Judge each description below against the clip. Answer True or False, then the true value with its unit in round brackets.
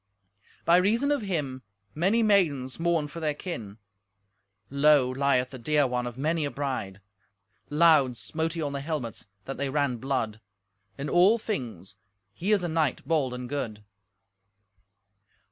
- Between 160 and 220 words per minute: False (150 wpm)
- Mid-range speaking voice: True (145 Hz)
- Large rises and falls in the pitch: False (4.7 semitones)